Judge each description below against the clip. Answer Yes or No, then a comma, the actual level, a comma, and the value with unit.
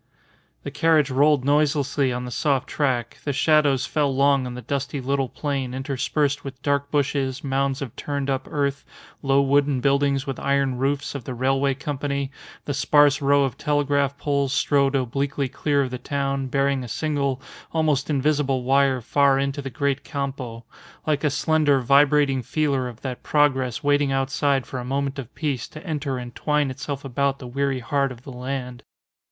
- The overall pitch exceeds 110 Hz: Yes, medium, 140 Hz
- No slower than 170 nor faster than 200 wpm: Yes, average, 175 wpm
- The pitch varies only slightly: Yes, narrow, 1.5 semitones